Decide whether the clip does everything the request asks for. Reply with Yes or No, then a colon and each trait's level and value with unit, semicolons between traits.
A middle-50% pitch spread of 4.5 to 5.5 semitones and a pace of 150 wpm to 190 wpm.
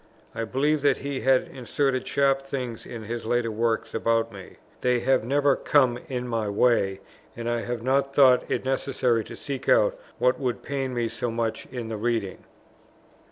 No: average, 2.9 semitones; average, 180 wpm